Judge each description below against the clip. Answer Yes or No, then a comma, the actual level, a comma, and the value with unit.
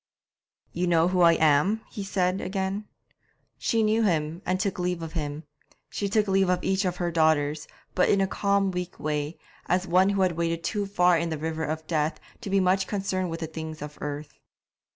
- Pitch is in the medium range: Yes, medium, 180 Hz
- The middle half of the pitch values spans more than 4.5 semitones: No, average, 3.3 semitones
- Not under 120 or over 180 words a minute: No, fast, 205 wpm